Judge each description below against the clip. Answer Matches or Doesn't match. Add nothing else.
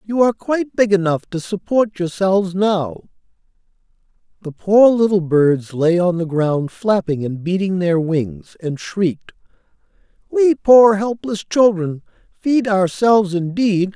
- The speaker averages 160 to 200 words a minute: Doesn't match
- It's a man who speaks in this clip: Matches